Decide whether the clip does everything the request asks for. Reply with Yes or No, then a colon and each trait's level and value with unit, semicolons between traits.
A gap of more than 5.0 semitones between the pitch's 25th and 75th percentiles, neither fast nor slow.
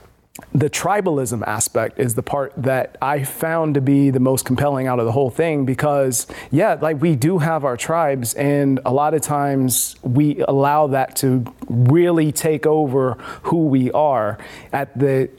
No: narrow, 2.6 semitones; average, 170 wpm